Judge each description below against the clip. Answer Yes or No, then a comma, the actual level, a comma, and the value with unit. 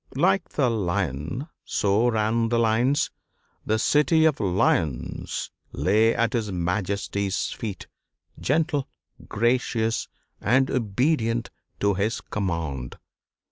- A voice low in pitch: Yes, low, 110 Hz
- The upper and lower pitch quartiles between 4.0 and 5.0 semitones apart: Yes, average, 4.3 semitones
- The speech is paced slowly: Yes, slow, 100 wpm